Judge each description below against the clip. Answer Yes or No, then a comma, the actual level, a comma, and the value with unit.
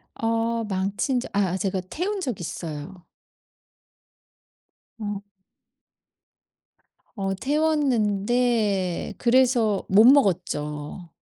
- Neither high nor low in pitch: No, high, 205 Hz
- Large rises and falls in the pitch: No, average, 4.5 semitones